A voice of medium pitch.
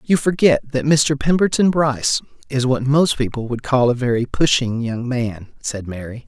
No: low, 130 Hz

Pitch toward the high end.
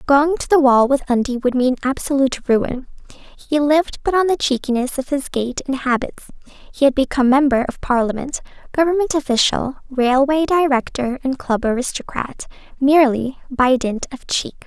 Yes: very high, 270 Hz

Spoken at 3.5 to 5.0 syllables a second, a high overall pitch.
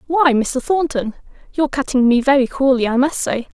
No: 5.4 syllables/s; very high, 270 Hz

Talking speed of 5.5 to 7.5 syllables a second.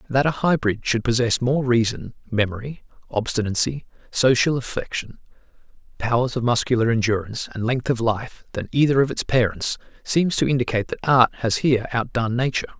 Yes: 5.7 syllables/s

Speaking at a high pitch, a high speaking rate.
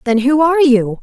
Yes: very high, 270 Hz; fast, 235 wpm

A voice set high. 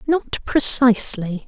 Yes: high, 245 Hz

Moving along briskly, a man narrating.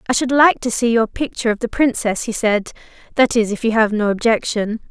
No: fast, 220 wpm; female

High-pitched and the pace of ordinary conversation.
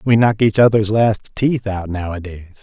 No: low, 105 Hz; average, 185 wpm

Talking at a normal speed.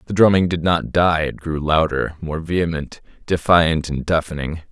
Yes: average, 165 wpm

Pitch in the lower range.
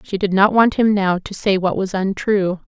No: high, 195 Hz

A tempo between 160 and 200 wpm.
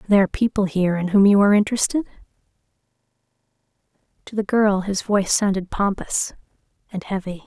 No: average, 145 wpm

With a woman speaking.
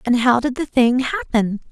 Yes: female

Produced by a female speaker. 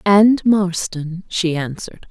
Yes: female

